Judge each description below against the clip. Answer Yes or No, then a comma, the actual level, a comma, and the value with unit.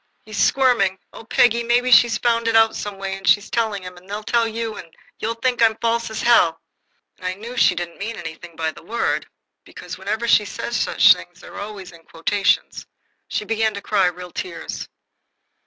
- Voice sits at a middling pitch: No, high, 215 Hz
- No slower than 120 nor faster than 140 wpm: No, average, 195 wpm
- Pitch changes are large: No, average, 3.3 semitones